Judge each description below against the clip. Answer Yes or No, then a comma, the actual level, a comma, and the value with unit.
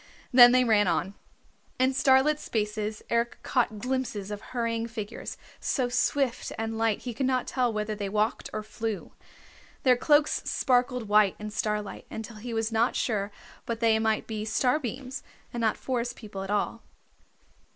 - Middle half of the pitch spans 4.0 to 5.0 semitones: No, average, 2.8 semitones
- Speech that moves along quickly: No, average, 160 wpm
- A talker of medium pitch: No, high, 225 Hz